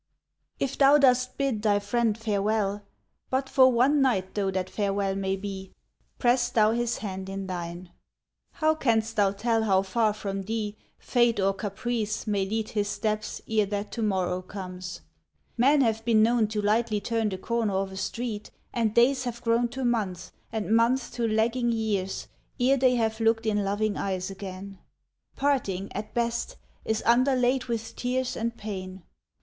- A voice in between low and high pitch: No, high, 220 Hz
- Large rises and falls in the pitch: No, average, 3.3 semitones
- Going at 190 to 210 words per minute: No, average, 165 wpm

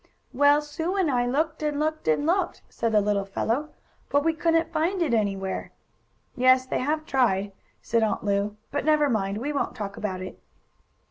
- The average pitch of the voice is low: No, very high, 260 Hz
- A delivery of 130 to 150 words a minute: No, average, 185 wpm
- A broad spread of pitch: Yes, wide, 6.7 semitones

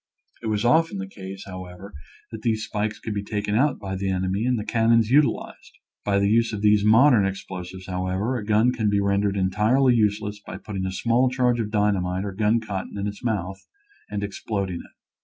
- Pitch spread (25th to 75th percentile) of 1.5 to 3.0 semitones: Yes, average, 2.7 semitones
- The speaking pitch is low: Yes, low, 105 Hz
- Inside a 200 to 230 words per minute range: Yes, fast, 205 wpm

